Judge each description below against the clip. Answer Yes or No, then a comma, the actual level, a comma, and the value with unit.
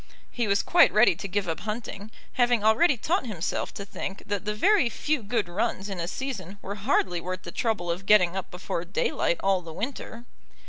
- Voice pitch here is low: No, high, 205 Hz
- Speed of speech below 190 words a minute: No, average, 200 wpm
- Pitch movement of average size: Yes, average, 4.3 semitones